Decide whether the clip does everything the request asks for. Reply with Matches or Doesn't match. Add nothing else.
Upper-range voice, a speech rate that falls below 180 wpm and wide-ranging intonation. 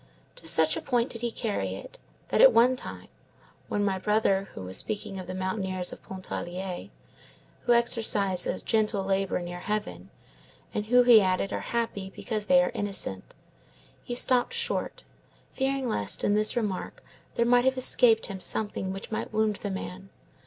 Doesn't match